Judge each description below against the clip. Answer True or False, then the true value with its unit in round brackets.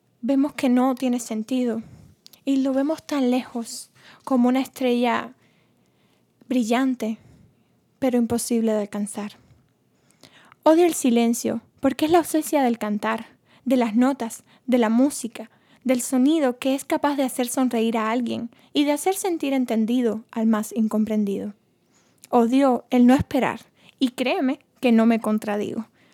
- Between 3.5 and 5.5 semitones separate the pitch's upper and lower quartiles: False (3.0 semitones)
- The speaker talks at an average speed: True (140 wpm)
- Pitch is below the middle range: False (245 Hz)